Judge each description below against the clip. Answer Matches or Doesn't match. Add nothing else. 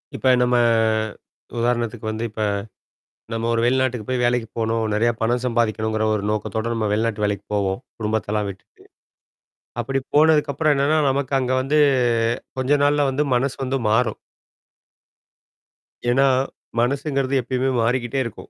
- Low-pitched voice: Matches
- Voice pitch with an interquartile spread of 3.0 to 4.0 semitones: Matches